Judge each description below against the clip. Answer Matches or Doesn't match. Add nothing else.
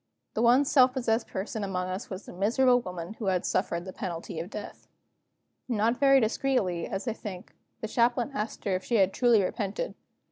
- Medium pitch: Doesn't match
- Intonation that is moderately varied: Matches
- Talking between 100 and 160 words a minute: Doesn't match